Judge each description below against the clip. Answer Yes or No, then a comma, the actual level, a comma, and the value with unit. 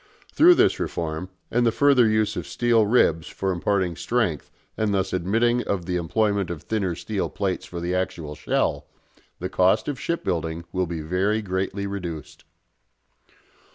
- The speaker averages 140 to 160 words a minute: Yes, average, 155 wpm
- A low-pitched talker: Yes, very low, 95 Hz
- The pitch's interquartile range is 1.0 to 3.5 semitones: No, average, 3.9 semitones